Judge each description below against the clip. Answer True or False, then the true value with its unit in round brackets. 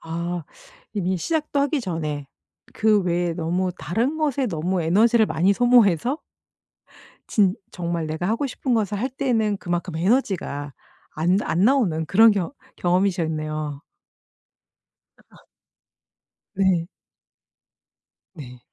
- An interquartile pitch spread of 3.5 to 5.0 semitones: False (5.5 semitones)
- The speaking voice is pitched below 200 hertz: True (185 Hz)